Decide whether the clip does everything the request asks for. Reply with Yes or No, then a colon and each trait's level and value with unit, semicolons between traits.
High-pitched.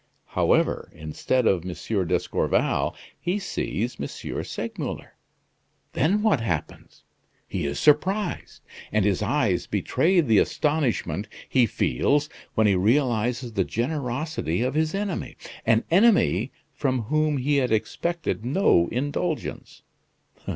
No: low, 130 Hz